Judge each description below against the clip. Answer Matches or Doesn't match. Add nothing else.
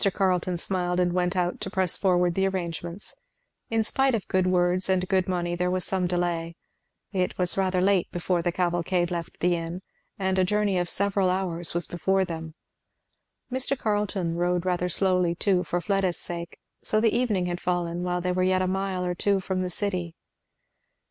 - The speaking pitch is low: Doesn't match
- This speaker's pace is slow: Doesn't match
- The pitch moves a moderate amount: Doesn't match